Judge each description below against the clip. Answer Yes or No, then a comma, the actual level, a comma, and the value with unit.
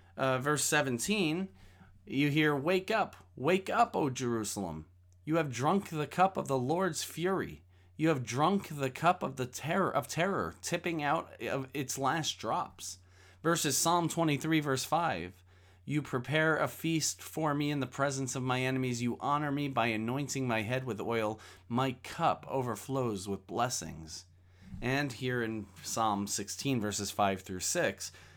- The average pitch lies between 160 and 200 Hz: No, low, 130 Hz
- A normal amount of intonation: No, wide, 6.8 semitones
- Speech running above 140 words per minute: Yes, average, 160 wpm